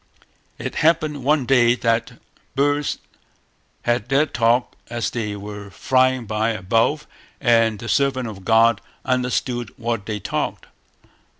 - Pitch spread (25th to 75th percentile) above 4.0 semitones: No, average, 2.8 semitones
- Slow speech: Yes, slow, 125 wpm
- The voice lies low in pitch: Yes, low, 120 Hz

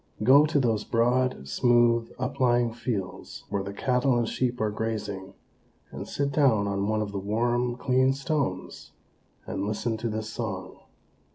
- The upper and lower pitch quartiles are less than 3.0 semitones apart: No, average, 3.4 semitones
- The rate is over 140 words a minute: Yes, average, 155 wpm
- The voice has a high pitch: No, low, 115 Hz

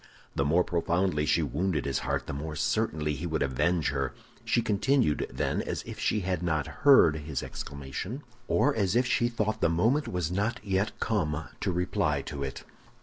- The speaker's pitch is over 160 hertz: No, very low, 85 Hz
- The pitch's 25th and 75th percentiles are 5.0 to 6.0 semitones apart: Yes, wide, 5.6 semitones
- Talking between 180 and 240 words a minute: Yes, average, 185 wpm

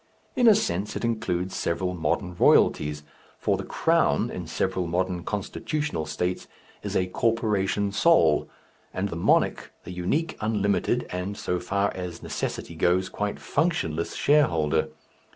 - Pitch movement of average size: Yes, average, 3.3 semitones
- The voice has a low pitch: Yes, very low, 95 Hz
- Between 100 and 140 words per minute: Yes, slow, 135 wpm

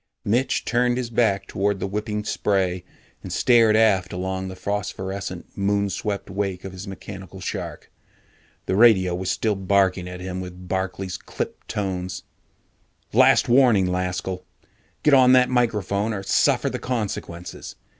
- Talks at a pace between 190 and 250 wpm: No, average, 145 wpm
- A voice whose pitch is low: Yes, very low, 95 Hz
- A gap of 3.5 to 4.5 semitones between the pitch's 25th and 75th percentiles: No, average, 2.8 semitones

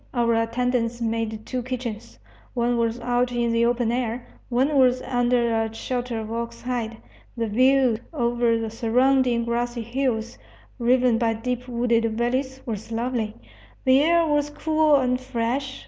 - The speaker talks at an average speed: Yes, average, 150 wpm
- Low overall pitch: No, high, 240 Hz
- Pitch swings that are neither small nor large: No, narrow, 1.8 semitones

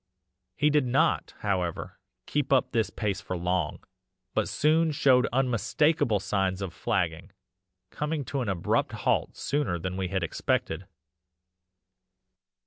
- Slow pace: Yes, slow, 130 wpm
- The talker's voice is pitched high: No, low, 105 Hz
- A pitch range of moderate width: No, wide, 7.1 semitones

